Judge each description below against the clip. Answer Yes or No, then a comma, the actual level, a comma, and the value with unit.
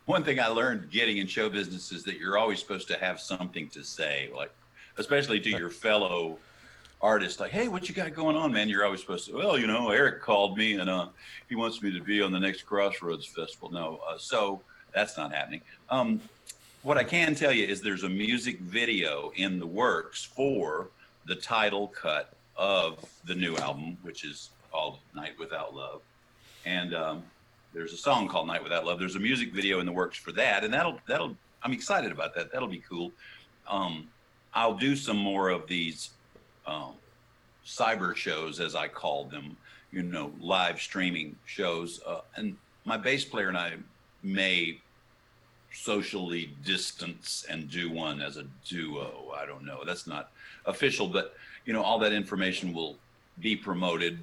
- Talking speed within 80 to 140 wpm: No, average, 185 wpm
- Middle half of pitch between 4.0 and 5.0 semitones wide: Yes, average, 4.4 semitones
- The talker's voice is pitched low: Yes, low, 100 Hz